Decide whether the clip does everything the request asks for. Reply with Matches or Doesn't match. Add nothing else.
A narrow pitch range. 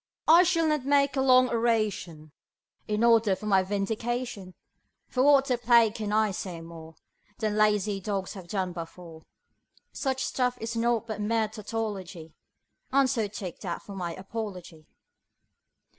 Doesn't match